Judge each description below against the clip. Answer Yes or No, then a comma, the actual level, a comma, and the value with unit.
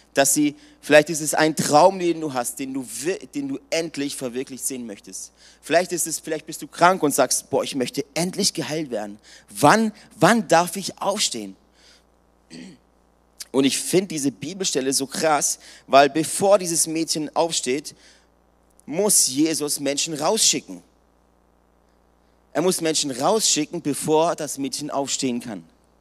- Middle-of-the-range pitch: Yes, medium, 155 Hz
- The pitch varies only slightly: No, average, 4.2 semitones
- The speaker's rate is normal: Yes, average, 145 wpm